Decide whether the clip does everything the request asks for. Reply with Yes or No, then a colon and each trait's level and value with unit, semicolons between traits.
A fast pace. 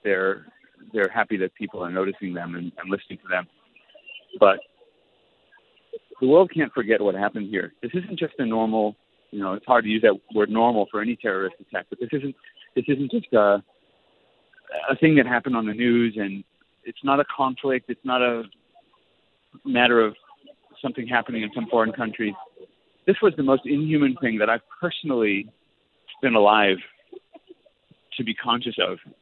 No: average, 175 wpm